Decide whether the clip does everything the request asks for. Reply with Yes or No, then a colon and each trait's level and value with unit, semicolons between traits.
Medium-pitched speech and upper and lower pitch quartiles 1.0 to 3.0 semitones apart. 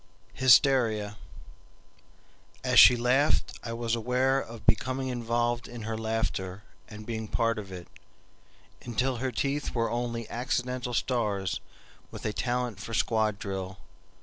No: low, 115 Hz; narrow, 2.6 semitones